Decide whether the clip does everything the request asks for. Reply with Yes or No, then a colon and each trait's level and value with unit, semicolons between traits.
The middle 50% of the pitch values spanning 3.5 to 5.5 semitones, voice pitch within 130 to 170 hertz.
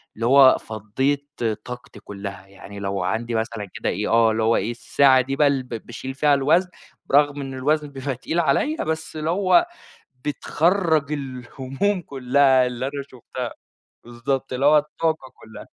Yes: average, 3.9 semitones; low, 135 Hz